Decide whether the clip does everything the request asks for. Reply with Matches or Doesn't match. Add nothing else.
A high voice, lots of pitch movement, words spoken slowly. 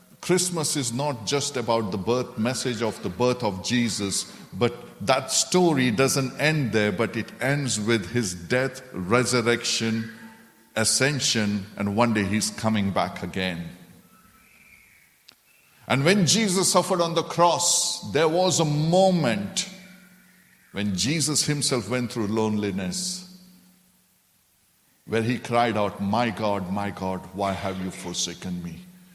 Doesn't match